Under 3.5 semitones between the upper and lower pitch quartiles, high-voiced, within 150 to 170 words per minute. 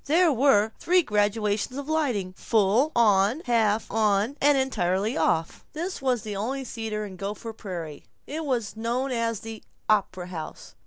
No: average, 4.7 semitones; high, 225 Hz; average, 155 wpm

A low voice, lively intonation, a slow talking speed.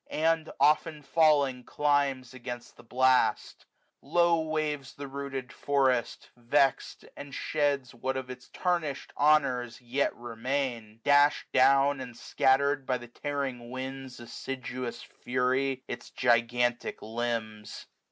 No: low, 130 Hz; average, 2.7 semitones; slow, 125 wpm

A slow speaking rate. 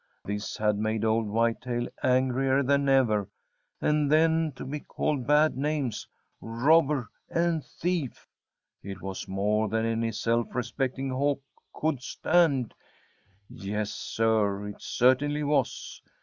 Yes: slow, 120 wpm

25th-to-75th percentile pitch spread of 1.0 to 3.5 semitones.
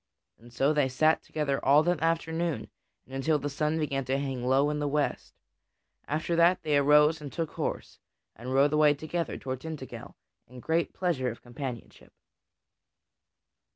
Yes: average, 3.0 semitones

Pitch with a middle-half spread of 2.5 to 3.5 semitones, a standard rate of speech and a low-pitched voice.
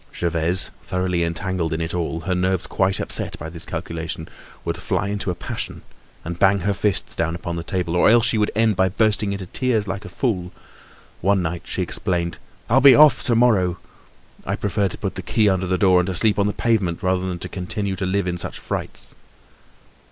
No: average, 2.8 semitones; fast, 210 wpm; very low, 95 Hz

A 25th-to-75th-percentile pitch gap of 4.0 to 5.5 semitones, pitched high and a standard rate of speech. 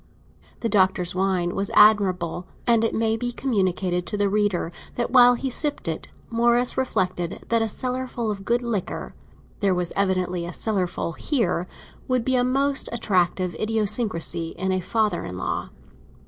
Yes: average, 4.6 semitones; high, 205 Hz; average, 160 wpm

